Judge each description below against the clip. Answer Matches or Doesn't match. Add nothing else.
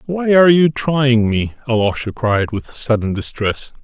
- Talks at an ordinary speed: Matches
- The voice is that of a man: Matches